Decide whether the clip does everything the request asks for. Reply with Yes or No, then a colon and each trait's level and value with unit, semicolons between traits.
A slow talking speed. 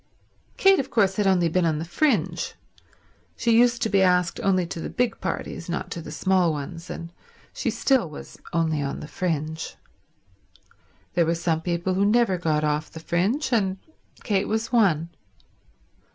No: average, 170 wpm